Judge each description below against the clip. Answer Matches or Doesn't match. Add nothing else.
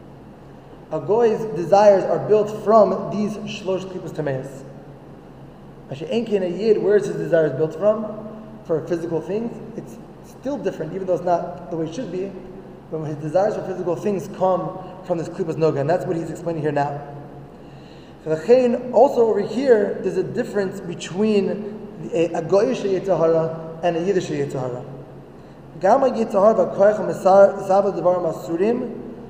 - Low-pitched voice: Doesn't match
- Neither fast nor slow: Matches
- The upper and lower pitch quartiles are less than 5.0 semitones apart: Matches